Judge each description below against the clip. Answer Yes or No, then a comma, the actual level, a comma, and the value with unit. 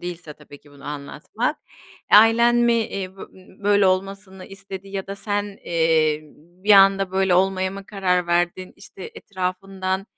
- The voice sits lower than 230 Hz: Yes, high, 190 Hz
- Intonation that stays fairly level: Yes, narrow, 1.8 semitones